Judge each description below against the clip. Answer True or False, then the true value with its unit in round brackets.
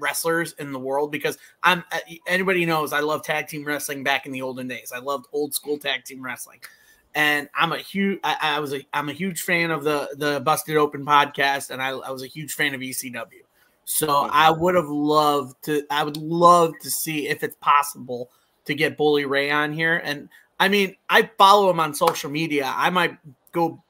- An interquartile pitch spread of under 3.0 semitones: True (2.5 semitones)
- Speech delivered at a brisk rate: True (210 wpm)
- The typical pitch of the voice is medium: True (150 Hz)